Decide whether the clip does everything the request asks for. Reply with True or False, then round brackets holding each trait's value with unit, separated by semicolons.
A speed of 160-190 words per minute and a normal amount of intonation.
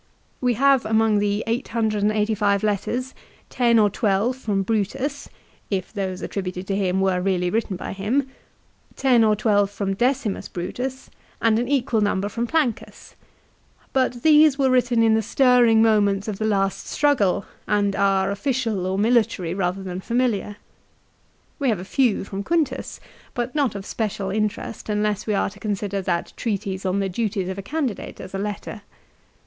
True (165 wpm; 3.6 semitones)